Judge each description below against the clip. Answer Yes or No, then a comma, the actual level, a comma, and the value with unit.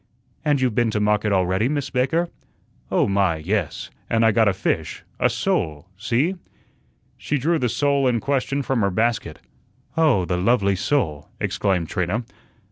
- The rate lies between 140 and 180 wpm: Yes, average, 160 wpm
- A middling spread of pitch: No, wide, 5.7 semitones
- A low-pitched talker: Yes, low, 115 Hz